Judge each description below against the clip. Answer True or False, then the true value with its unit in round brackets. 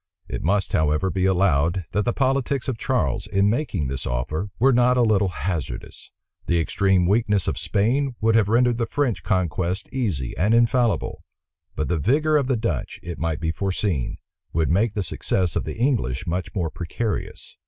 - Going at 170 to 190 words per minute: True (180 wpm)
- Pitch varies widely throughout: True (5.8 semitones)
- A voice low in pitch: True (100 Hz)